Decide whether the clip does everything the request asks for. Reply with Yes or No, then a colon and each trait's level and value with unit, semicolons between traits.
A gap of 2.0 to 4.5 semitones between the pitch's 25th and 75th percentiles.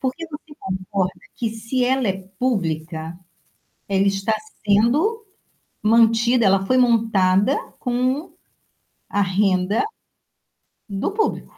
No: average, 4.9 semitones